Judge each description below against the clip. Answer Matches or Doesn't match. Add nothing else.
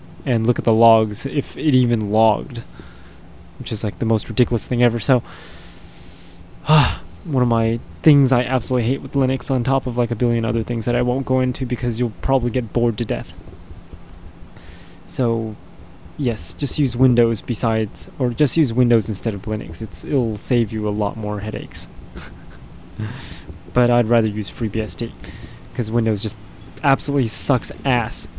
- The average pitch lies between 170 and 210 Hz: Doesn't match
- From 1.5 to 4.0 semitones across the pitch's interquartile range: Doesn't match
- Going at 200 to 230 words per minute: Doesn't match